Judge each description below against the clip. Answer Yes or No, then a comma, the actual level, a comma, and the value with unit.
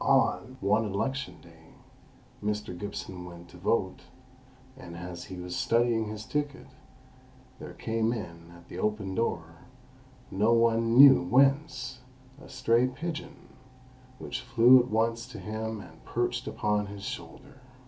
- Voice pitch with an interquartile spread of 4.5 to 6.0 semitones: Yes, average, 5.0 semitones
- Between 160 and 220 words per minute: No, average, 140 wpm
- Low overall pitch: Yes, low, 110 Hz